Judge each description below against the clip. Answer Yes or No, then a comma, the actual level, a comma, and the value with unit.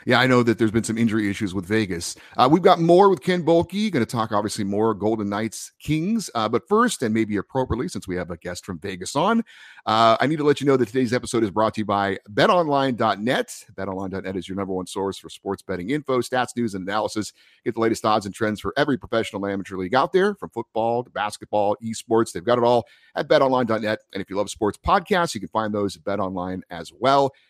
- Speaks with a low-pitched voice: Yes, low, 110 Hz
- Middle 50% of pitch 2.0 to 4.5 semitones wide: No, average, 4.9 semitones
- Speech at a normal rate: No, fast, 235 wpm